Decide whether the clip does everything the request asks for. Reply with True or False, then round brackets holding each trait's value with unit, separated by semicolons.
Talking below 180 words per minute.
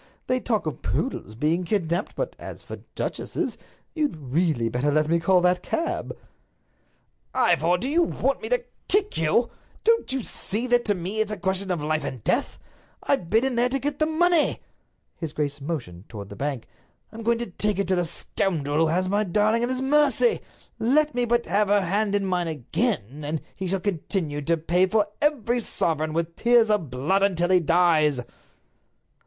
False (190 wpm)